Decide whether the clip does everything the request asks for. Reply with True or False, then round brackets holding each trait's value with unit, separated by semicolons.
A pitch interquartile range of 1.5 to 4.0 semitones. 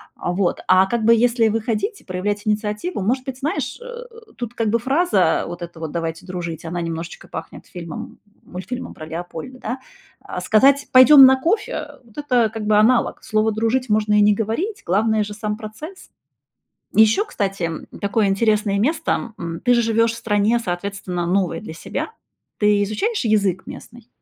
False (4.4 semitones)